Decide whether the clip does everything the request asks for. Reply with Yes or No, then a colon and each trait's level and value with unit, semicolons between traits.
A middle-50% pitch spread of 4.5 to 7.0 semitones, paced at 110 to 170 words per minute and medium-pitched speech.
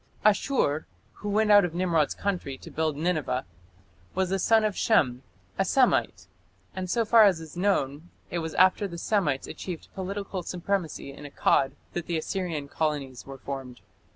Yes: average, 5.3 semitones; average, 165 wpm; medium, 175 Hz